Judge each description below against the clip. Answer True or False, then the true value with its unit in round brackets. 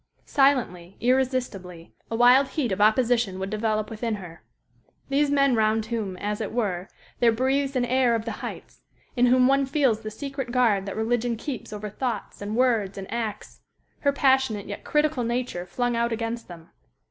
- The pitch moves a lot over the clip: False (3.5 semitones)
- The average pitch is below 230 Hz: False (235 Hz)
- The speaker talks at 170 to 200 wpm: True (175 wpm)